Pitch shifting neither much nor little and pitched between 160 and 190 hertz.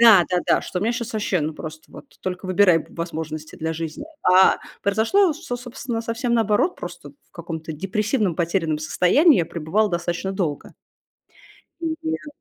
No: wide, 5.7 semitones; medium, 185 Hz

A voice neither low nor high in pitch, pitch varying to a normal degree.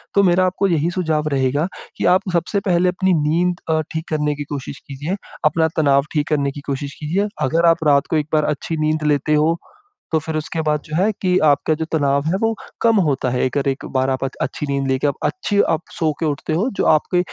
Yes: medium, 155 Hz; average, 3.3 semitones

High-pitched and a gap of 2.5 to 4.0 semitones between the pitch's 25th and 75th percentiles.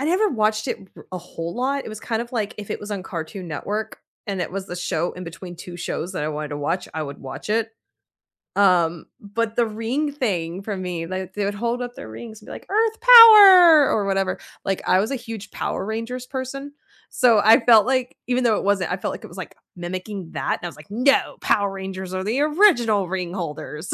No: high, 205 Hz; average, 5.1 semitones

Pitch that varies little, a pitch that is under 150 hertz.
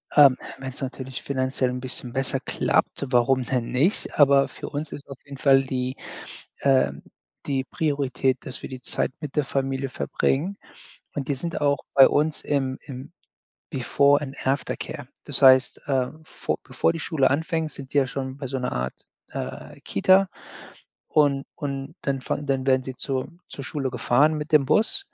Yes: narrow, 1.7 semitones; low, 135 Hz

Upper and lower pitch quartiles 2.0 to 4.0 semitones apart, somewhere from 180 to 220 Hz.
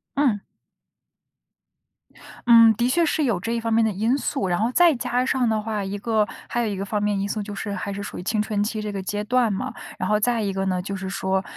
Yes: average, 2.8 semitones; high, 215 Hz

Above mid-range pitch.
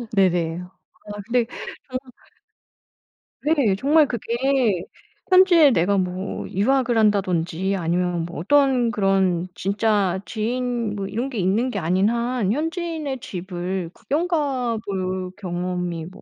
Yes: high, 205 Hz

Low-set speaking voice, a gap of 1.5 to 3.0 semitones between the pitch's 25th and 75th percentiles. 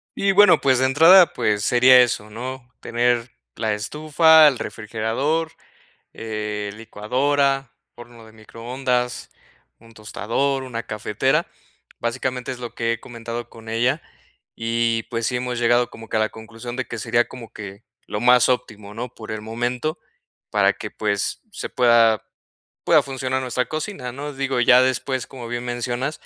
Yes: low, 120 Hz; narrow, 2.5 semitones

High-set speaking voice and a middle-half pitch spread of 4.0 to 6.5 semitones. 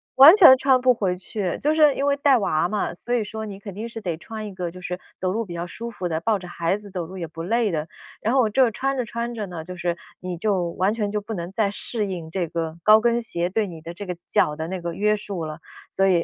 Yes: high, 200 Hz; average, 4.5 semitones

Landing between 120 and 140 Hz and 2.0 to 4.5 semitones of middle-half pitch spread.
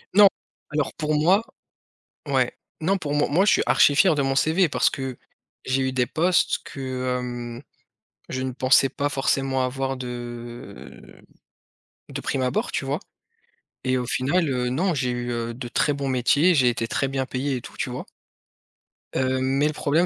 Yes: low, 135 Hz; average, 2.7 semitones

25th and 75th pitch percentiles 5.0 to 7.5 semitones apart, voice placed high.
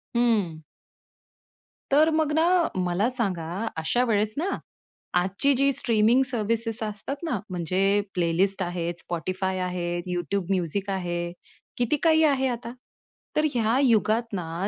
Yes: wide, 5.6 semitones; high, 210 Hz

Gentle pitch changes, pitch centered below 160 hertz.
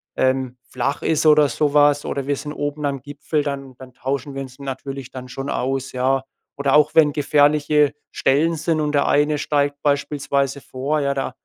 Yes: narrow, 1.6 semitones; medium, 140 Hz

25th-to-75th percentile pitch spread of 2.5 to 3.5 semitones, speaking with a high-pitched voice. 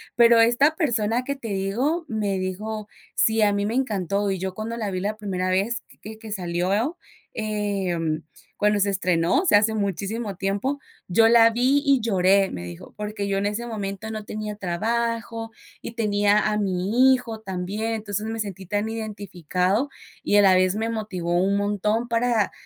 Yes: average, 2.8 semitones; high, 210 Hz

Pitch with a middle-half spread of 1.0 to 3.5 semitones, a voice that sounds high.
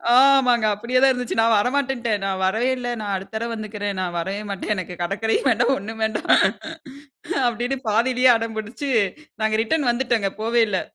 Yes: average, 3.2 semitones; high, 225 Hz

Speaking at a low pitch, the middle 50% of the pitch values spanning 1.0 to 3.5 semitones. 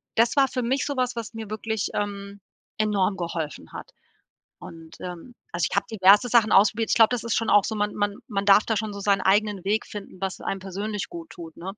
No: high, 210 Hz; narrow, 2.5 semitones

